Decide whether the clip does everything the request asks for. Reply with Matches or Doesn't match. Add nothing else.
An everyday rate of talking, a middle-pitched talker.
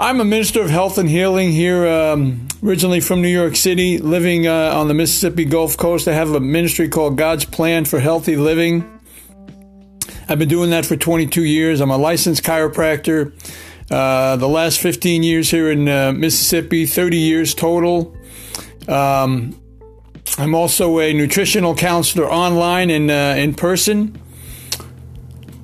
Matches